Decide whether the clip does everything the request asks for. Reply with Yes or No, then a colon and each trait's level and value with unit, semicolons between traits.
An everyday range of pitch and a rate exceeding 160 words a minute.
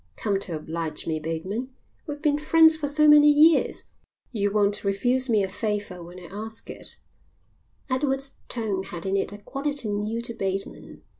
No: wide, 6.1 semitones; average, 170 wpm